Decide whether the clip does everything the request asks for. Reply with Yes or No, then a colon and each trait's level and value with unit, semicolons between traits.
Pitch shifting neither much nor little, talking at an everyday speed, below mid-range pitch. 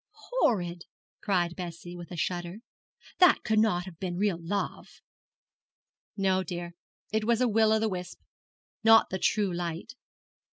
No: average, 3.7 semitones; average, 150 wpm; medium, 185 Hz